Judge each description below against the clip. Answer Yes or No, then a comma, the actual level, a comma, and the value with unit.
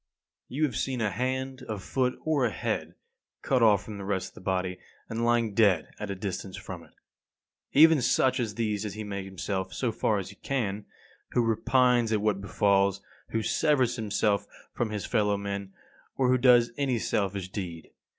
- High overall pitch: No, low, 105 Hz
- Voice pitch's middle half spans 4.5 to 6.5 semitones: No, average, 4.0 semitones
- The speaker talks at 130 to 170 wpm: No, average, 190 wpm